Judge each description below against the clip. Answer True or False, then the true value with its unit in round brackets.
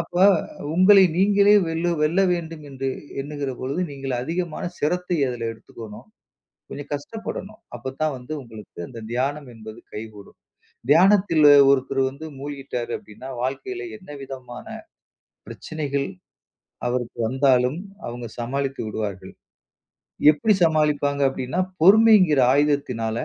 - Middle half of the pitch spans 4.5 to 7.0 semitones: True (4.9 semitones)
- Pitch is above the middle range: False (140 Hz)